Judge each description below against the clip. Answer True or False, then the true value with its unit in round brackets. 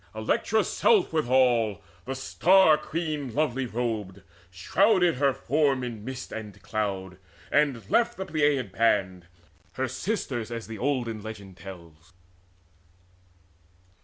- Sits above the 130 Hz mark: False (120 Hz)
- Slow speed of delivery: True (115 wpm)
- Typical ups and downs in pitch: False (5.9 semitones)